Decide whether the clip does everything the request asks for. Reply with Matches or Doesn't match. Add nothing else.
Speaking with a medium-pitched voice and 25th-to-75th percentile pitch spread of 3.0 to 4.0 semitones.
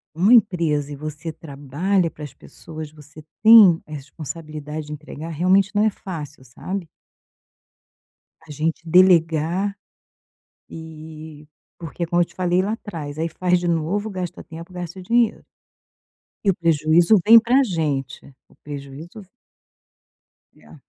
Matches